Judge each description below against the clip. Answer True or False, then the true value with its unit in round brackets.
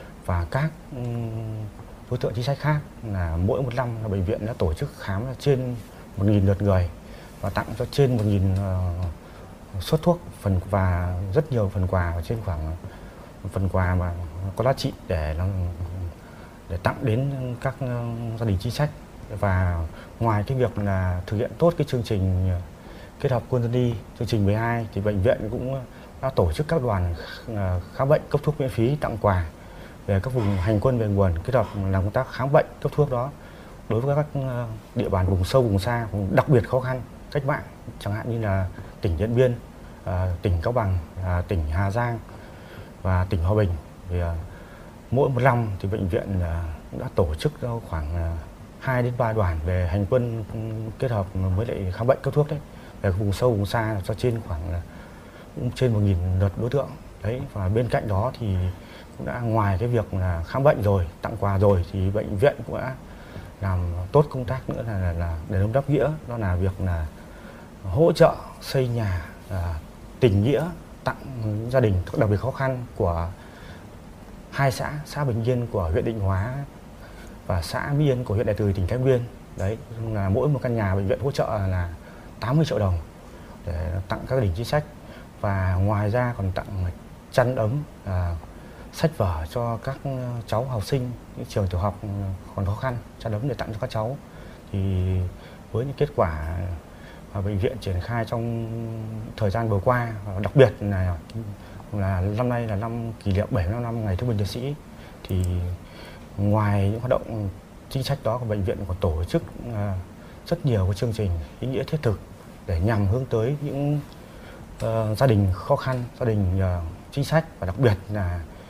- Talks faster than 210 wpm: False (190 wpm)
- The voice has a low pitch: True (105 Hz)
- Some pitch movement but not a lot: True (4.8 semitones)